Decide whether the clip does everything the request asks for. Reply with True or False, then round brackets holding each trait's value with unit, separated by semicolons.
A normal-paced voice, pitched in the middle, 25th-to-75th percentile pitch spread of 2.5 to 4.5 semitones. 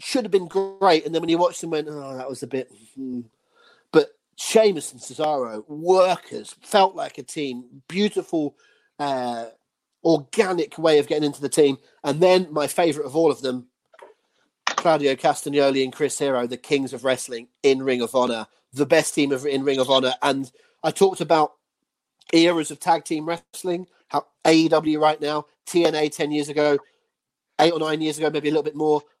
True (185 wpm; 150 Hz; 3.5 semitones)